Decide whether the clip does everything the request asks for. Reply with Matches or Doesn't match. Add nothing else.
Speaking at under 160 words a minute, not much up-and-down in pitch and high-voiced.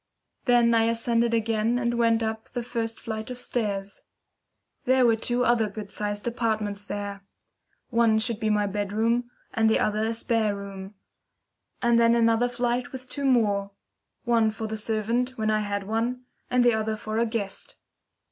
Doesn't match